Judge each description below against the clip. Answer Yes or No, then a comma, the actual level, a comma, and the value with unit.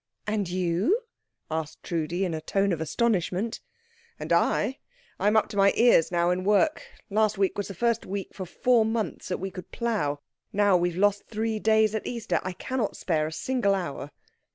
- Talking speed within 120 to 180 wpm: No, average, 200 wpm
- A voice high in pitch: Yes, high, 200 Hz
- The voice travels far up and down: No, average, 3.7 semitones